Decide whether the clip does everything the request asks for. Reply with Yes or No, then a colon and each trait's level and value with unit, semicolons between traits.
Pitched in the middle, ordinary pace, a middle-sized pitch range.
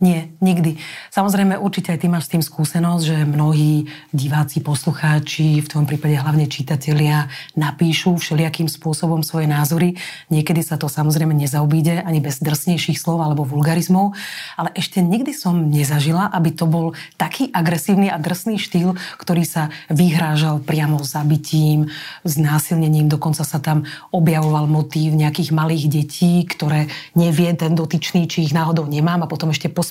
No: medium, 160 Hz; average, 150 wpm; narrow, 2.1 semitones